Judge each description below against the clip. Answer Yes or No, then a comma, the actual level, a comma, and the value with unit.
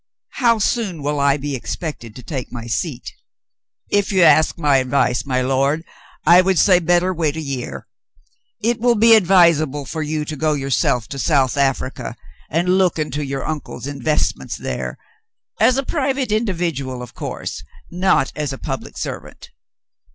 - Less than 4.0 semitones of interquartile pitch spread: No, average, 5.1 semitones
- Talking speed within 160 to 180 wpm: Yes, average, 165 wpm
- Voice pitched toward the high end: No, medium, 155 Hz